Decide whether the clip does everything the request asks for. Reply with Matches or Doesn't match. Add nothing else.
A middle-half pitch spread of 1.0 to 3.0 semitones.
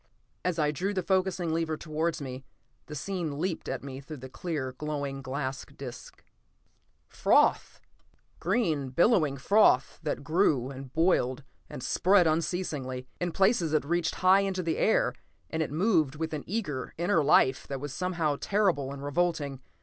Doesn't match